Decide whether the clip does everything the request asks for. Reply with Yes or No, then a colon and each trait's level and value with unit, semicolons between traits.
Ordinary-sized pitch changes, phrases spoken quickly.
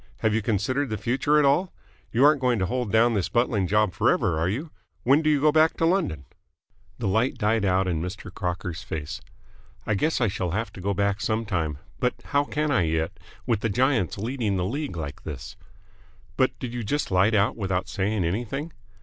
No: wide, 5.7 semitones; fast, 210 wpm